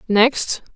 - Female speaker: Yes, female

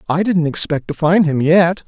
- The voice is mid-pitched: Yes, medium, 165 Hz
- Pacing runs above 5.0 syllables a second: No, 4.7 syllables/s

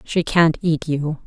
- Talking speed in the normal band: Yes, average, 190 wpm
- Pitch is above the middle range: No, medium, 160 Hz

